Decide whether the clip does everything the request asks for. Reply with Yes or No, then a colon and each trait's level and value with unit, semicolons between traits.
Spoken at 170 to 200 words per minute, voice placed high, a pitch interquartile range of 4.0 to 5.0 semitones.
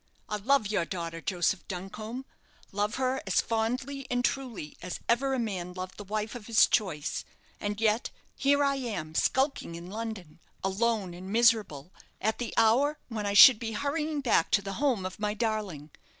Yes: average, 180 wpm; high, 215 Hz; average, 4.7 semitones